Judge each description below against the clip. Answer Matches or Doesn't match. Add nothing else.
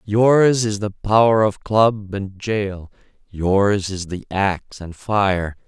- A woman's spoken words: Doesn't match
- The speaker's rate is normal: Matches